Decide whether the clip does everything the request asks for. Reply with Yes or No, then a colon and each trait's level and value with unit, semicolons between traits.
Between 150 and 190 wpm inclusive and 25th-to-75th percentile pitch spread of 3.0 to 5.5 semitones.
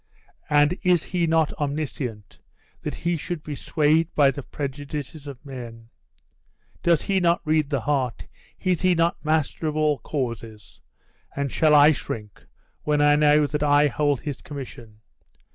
No: average, 155 wpm; narrow, 2.5 semitones